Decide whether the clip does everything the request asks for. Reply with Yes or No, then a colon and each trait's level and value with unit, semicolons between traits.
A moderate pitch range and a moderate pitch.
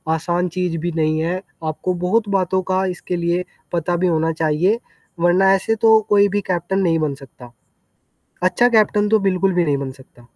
Yes: average, 3.1 semitones; medium, 180 Hz